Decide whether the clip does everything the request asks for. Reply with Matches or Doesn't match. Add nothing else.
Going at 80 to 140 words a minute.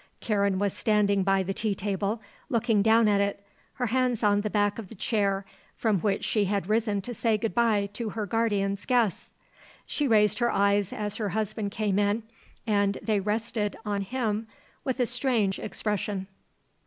Doesn't match